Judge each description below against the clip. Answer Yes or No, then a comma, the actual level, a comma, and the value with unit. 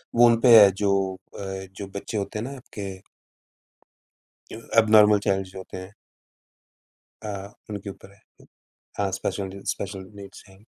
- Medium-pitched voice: No, low, 100 Hz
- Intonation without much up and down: Yes, narrow, 1.8 semitones